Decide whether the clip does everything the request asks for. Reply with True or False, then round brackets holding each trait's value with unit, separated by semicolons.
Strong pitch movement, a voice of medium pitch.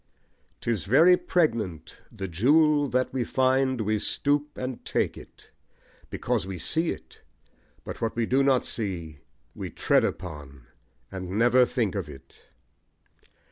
False (6.2 semitones; 115 Hz)